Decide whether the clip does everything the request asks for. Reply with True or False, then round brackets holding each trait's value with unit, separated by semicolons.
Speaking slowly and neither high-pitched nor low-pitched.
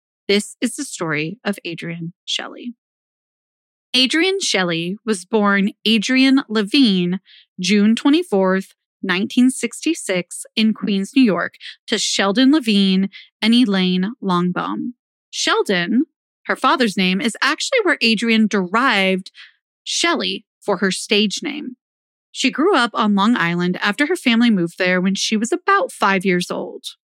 False (130 wpm; 220 Hz)